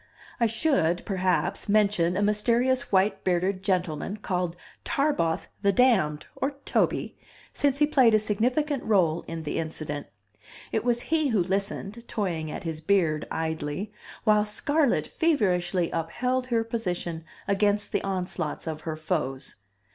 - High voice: Yes, high, 195 Hz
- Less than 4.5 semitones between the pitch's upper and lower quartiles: No, wide, 5.6 semitones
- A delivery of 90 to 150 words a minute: Yes, average, 140 wpm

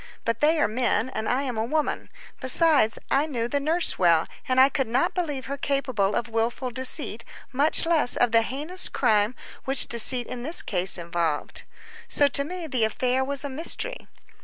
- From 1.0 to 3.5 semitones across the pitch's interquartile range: No, average, 3.9 semitones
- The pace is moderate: Yes, average, 185 wpm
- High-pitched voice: Yes, very high, 260 Hz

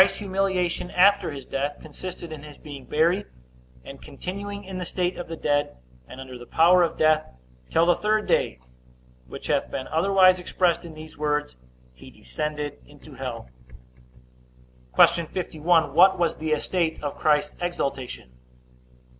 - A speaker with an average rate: Yes, average, 155 wpm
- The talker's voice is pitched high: No, medium, 160 Hz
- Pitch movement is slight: No, average, 3.7 semitones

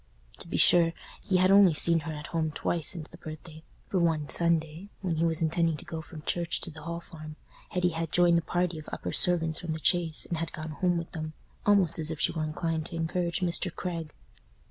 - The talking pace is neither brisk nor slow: No, fast, 225 wpm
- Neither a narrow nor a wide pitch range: No, narrow, 1.8 semitones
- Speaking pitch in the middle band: Yes, medium, 165 Hz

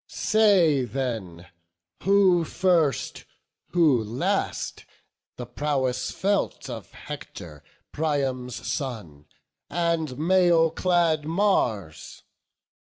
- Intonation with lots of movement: Yes, wide, 5.8 semitones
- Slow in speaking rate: Yes, slow, 80 wpm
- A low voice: No, medium, 150 Hz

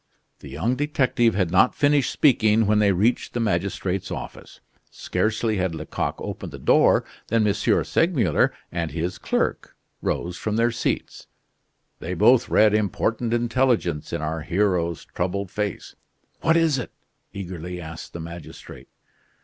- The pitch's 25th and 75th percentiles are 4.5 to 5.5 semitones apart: Yes, average, 4.9 semitones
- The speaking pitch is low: Yes, low, 105 Hz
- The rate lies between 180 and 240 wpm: No, average, 140 wpm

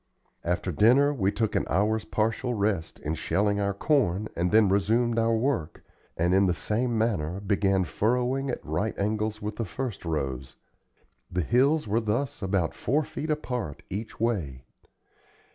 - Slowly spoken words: No, average, 160 wpm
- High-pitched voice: No, low, 105 Hz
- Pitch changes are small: No, average, 4.2 semitones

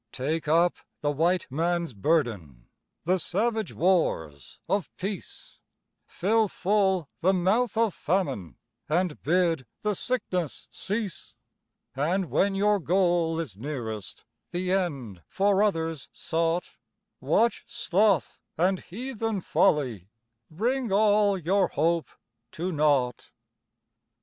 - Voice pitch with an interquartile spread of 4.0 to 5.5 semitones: Yes, average, 4.6 semitones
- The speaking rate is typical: No, slow, 110 wpm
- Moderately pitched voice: Yes, medium, 175 Hz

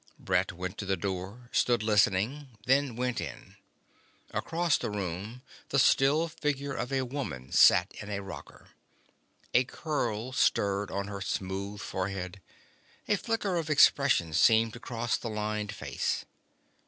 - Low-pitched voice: Yes, low, 110 Hz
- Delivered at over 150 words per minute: No, average, 140 wpm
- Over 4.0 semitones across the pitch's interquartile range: Yes, wide, 5.6 semitones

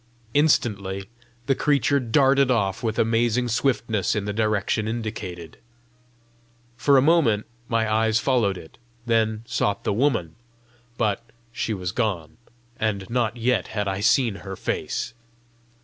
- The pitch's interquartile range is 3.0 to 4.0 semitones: Yes, average, 3.5 semitones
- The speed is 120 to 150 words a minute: Yes, slow, 135 wpm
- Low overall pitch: Yes, low, 110 Hz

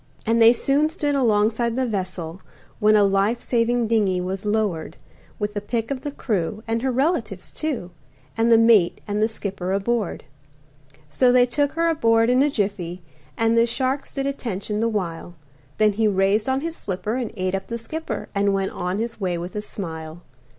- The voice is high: Yes, high, 220 Hz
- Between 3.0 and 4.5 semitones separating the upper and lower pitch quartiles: Yes, average, 3.8 semitones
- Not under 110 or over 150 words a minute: No, average, 190 wpm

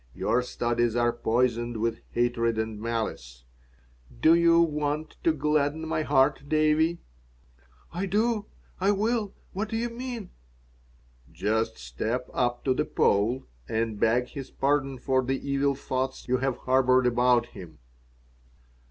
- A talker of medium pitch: No, low, 130 Hz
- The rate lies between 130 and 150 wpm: Yes, slow, 135 wpm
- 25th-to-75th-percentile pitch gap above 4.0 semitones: Yes, average, 4.7 semitones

